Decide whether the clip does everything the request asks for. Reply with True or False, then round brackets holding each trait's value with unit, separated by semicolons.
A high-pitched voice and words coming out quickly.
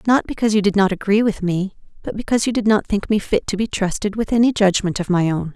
True (205 Hz; 260 wpm)